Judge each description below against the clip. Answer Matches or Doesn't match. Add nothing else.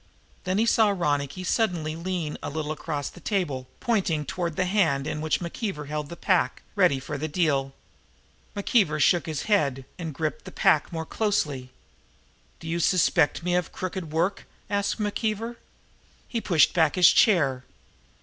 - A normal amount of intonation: Matches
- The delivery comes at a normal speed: Matches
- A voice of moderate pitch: Matches